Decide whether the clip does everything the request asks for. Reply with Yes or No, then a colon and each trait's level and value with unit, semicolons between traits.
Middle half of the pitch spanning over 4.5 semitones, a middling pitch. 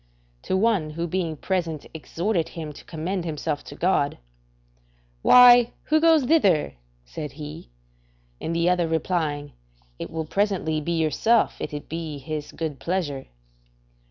No: average, 3.6 semitones; medium, 165 Hz